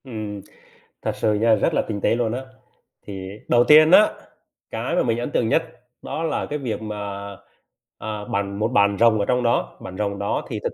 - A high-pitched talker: No, low, 110 Hz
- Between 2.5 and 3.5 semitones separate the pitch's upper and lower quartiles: Yes, average, 3.0 semitones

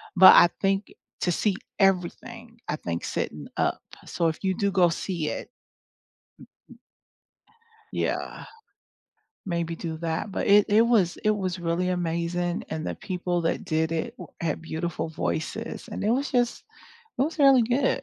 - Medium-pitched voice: Yes, medium, 180 Hz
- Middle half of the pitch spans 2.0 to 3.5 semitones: No, average, 4.2 semitones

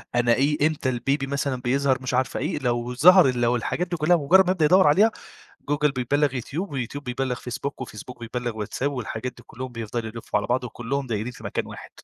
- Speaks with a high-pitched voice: No, low, 130 Hz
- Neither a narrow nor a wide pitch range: Yes, average, 3.2 semitones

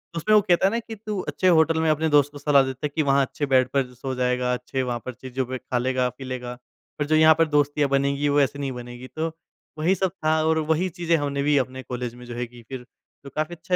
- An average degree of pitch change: Yes, average, 3.7 semitones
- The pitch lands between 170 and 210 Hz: No, medium, 140 Hz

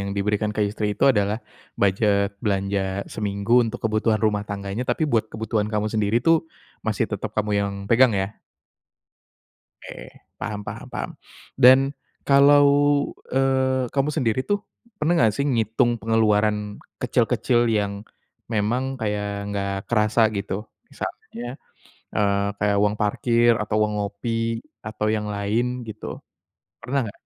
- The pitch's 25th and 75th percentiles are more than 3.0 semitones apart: No, narrow, 2.5 semitones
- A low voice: Yes, low, 105 Hz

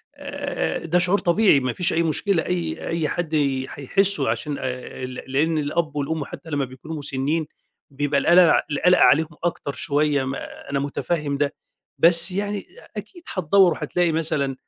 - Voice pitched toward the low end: No, medium, 155 Hz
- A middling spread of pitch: Yes, average, 3.9 semitones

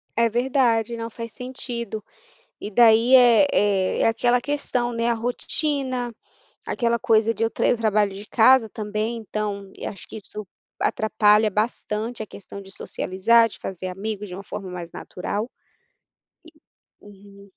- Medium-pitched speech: No, high, 220 Hz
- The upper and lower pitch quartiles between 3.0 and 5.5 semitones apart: No, narrow, 2.6 semitones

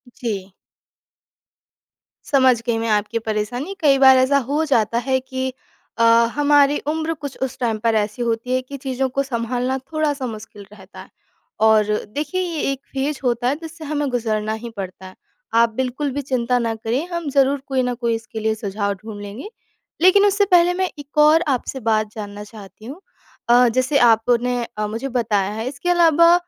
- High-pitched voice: Yes, very high, 250 Hz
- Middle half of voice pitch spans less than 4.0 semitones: No, average, 4.4 semitones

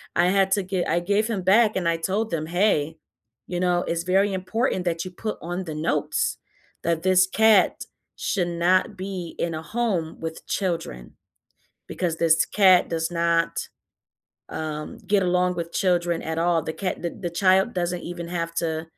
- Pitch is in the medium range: Yes, medium, 175 Hz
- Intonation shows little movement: Yes, narrow, 2.2 semitones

